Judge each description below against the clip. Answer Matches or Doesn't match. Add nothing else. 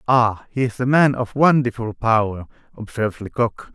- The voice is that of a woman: Doesn't match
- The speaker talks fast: Doesn't match